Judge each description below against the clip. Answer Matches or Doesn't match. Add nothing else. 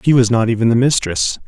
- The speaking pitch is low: Matches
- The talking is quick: Matches